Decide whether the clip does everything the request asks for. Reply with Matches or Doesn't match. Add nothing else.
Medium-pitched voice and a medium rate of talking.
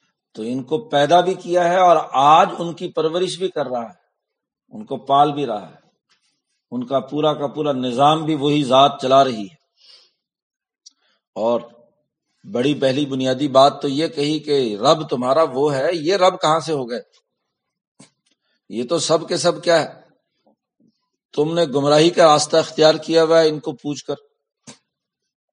Matches